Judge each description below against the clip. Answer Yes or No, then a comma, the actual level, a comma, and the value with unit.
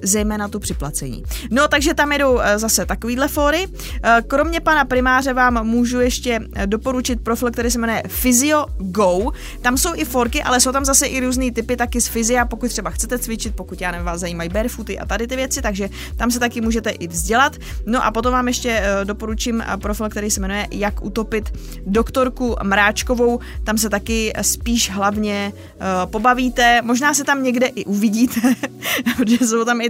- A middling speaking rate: No, fast, 175 wpm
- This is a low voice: No, high, 235 Hz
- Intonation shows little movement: No, average, 3.1 semitones